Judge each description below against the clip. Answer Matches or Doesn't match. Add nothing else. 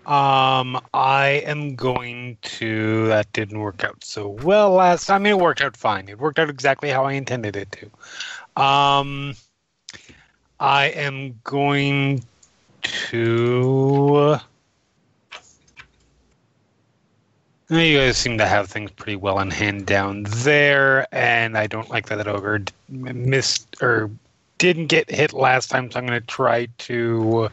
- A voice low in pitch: Matches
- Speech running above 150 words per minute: Doesn't match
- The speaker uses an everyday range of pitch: Matches